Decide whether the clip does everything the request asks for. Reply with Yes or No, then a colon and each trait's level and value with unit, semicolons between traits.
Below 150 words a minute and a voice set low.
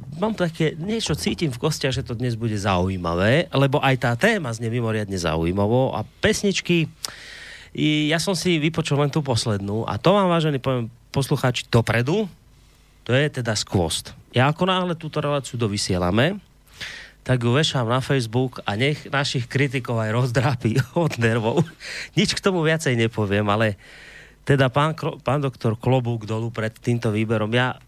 No: average, 155 wpm; low, 130 Hz